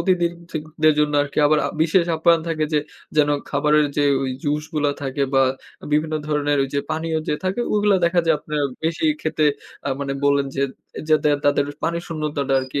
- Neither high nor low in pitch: Yes, medium, 150 Hz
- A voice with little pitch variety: Yes, narrow, 2.0 semitones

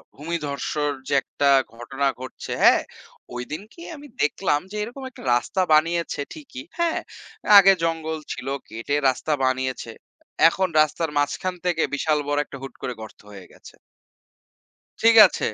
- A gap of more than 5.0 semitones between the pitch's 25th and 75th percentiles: Yes, wide, 5.4 semitones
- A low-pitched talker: No, medium, 155 Hz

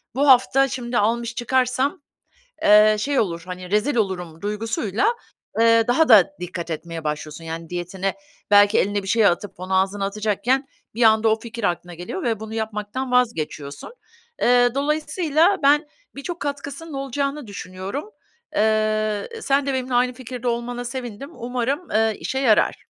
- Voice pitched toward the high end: Yes, high, 225 Hz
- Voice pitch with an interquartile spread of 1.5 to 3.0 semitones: No, average, 4.7 semitones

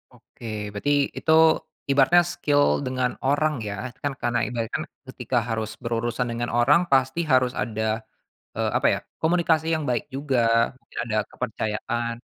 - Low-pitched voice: Yes, low, 125 Hz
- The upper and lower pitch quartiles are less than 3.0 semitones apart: No, average, 3.5 semitones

